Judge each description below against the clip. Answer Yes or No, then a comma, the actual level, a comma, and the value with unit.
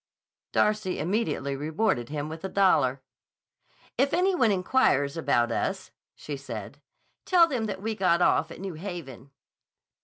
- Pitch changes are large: Yes, wide, 7.3 semitones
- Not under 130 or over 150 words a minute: Yes, average, 145 wpm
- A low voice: No, medium, 175 Hz